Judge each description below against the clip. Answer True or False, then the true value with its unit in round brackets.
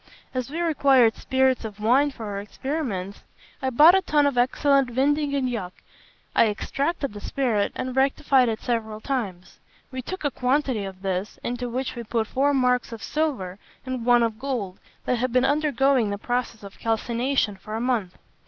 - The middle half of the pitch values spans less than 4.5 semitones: True (3.9 semitones)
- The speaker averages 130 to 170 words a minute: False (180 wpm)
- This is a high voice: True (250 Hz)